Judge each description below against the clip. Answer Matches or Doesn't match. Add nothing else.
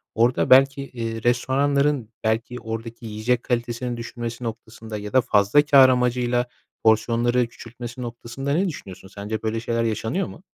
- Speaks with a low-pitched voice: Matches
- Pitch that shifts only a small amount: Matches